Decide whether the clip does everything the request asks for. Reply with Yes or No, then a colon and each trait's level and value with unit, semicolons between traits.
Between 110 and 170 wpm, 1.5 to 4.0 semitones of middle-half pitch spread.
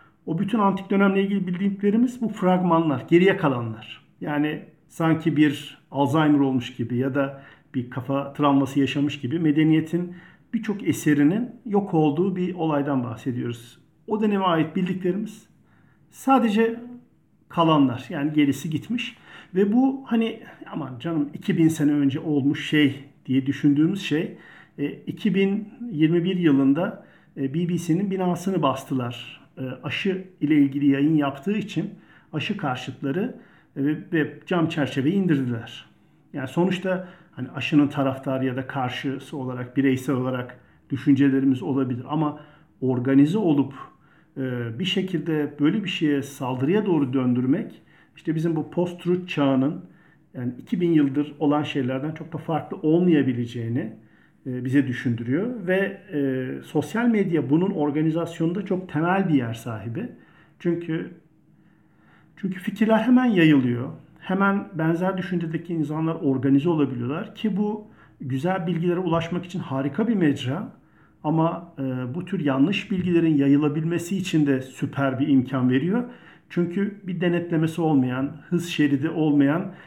No: average, 120 wpm; average, 4.6 semitones